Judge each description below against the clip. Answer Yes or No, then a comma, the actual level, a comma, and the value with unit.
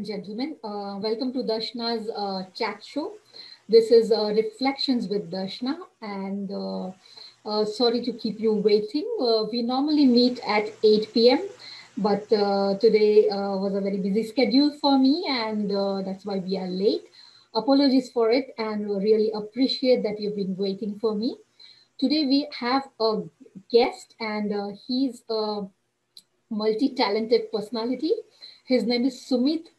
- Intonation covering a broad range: No, average, 3.7 semitones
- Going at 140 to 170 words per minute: Yes, average, 150 wpm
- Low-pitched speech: No, high, 225 Hz